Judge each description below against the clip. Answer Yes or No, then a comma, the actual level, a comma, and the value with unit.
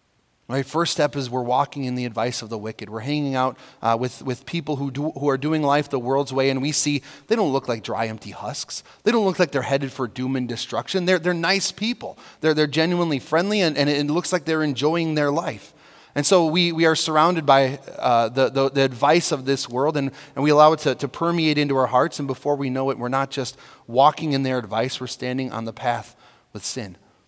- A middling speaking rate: No, fast, 240 wpm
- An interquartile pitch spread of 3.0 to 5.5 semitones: Yes, average, 3.5 semitones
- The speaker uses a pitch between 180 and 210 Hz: No, low, 135 Hz